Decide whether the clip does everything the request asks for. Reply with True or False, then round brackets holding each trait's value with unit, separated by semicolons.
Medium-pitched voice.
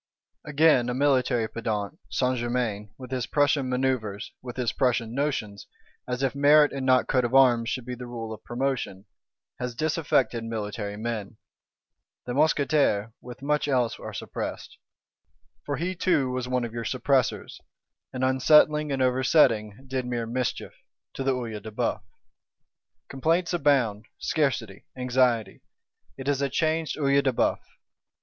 False (125 Hz)